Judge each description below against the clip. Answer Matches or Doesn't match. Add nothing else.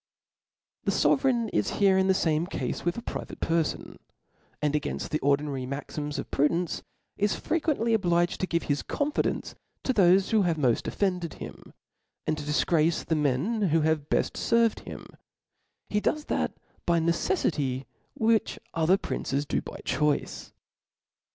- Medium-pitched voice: Matches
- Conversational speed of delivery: Matches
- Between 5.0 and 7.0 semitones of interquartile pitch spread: Matches